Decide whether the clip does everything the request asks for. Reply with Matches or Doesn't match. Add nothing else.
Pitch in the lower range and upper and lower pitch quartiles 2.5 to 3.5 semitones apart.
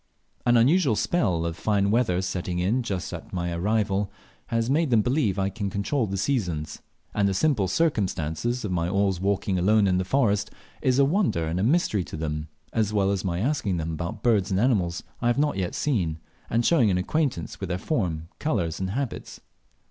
Doesn't match